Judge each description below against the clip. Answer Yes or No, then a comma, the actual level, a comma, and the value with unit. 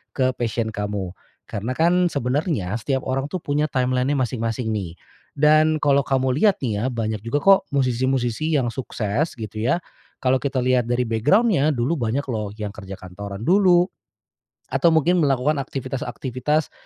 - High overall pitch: No, low, 130 Hz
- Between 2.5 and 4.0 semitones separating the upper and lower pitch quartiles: No, average, 4.6 semitones